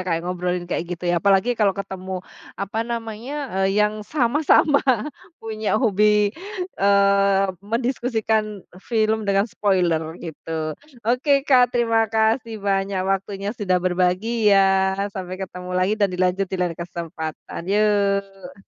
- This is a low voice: No, high, 200 Hz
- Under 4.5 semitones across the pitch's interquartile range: Yes, average, 3.1 semitones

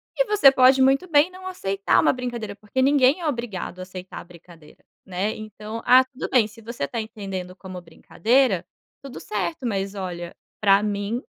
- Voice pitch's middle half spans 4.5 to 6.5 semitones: Yes, wide, 5.4 semitones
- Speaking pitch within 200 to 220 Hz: Yes, high, 215 Hz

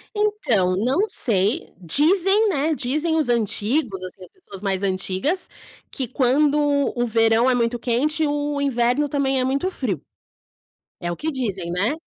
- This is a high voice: Yes, very high, 255 Hz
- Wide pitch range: Yes, wide, 6.0 semitones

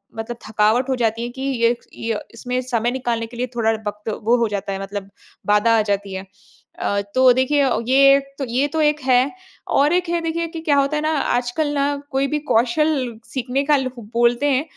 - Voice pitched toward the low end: No, very high, 250 Hz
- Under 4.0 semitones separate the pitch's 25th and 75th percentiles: Yes, average, 3.4 semitones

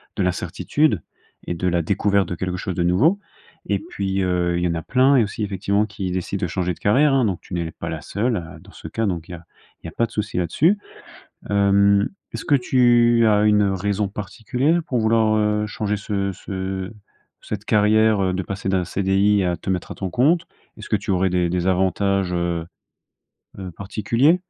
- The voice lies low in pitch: Yes, low, 100 Hz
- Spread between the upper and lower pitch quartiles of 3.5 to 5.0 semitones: No, average, 3.0 semitones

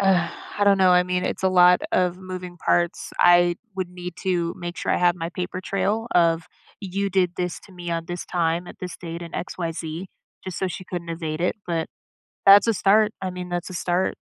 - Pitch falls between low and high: Yes, medium, 180 Hz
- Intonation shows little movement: Yes, narrow, 1.3 semitones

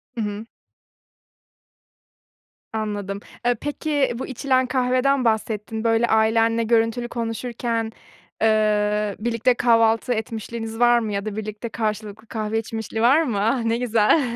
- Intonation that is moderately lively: No, narrow, 1.8 semitones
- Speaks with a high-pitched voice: Yes, high, 225 Hz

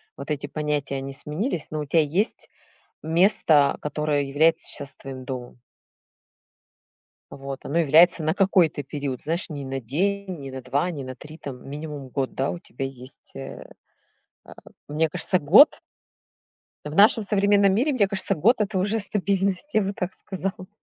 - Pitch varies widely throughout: Yes, wide, 5.7 semitones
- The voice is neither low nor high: Yes, medium, 155 Hz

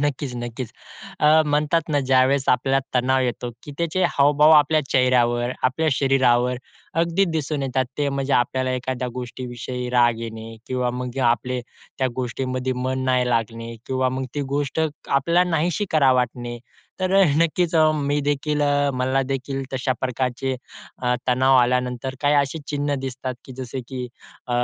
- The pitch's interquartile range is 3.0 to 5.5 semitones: No, narrow, 2.5 semitones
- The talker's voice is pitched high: No, low, 130 Hz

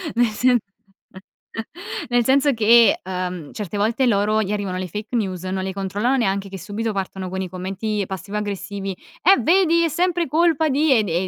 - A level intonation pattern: No, average, 4.6 semitones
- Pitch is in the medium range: No, high, 210 Hz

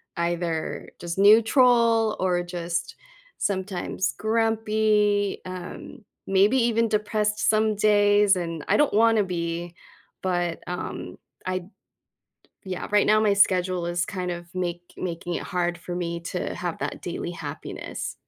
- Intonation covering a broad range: No, average, 3.5 semitones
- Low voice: No, high, 190 Hz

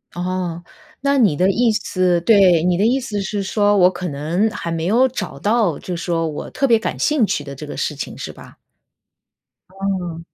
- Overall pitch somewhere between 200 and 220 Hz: No, medium, 185 Hz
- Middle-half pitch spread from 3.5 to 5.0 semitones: Yes, average, 4.2 semitones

